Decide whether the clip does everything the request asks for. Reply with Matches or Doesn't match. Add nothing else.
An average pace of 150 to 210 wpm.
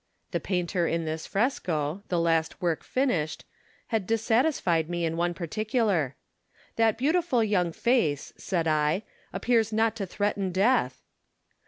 Doesn't match